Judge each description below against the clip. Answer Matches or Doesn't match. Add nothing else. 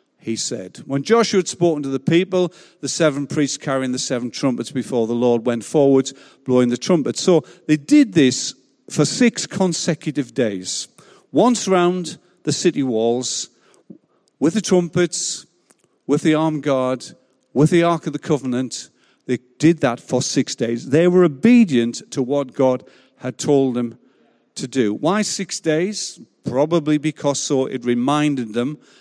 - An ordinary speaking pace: Matches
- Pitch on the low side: Doesn't match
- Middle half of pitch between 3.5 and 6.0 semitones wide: Matches